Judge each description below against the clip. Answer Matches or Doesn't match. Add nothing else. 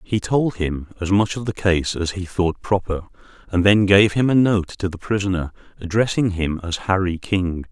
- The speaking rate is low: Doesn't match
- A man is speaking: Matches